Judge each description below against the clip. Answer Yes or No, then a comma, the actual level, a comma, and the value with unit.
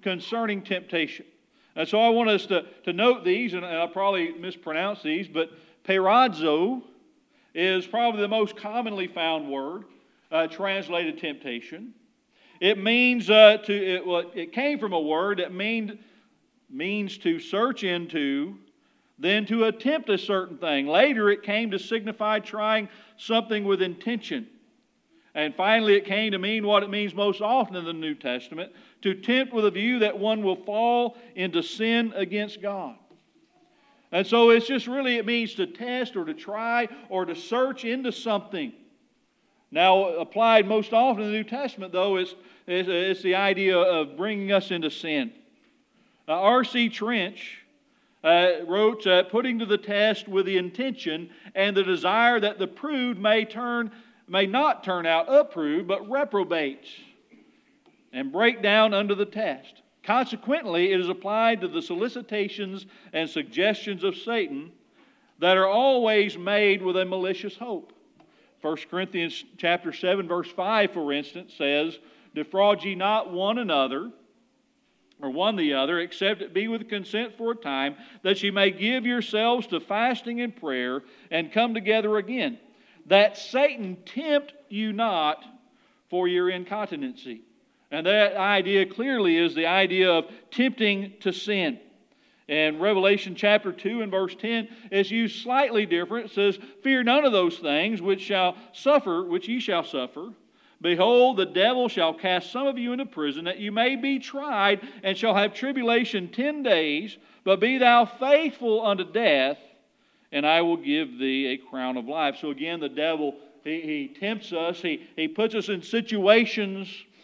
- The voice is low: No, high, 210 Hz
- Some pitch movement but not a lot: Yes, average, 4.9 semitones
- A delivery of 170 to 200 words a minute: No, average, 160 wpm